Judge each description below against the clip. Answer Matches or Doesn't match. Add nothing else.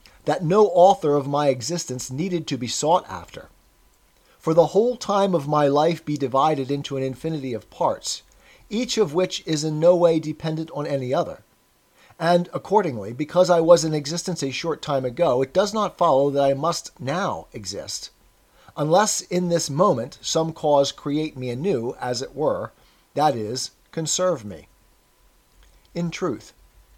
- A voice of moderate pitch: Matches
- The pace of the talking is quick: Doesn't match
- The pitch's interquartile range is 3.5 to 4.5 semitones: Matches